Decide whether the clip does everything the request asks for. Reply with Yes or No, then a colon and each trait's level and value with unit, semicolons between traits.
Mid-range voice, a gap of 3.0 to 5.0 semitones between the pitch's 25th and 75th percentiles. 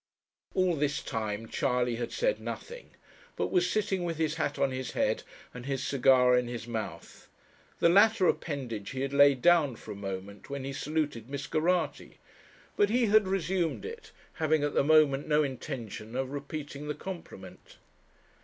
No: medium, 145 Hz; wide, 5.4 semitones